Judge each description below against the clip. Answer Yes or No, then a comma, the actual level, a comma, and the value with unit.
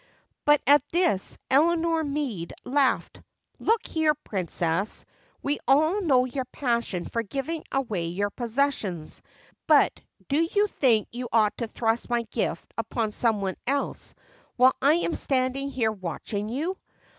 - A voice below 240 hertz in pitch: No, very high, 255 Hz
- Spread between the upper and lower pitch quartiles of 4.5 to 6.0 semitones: Yes, average, 5.3 semitones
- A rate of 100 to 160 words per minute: Yes, average, 140 wpm